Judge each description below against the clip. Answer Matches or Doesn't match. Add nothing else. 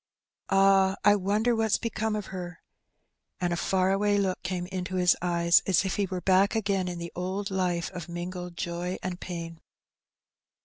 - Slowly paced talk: Doesn't match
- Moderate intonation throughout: Doesn't match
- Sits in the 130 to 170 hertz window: Doesn't match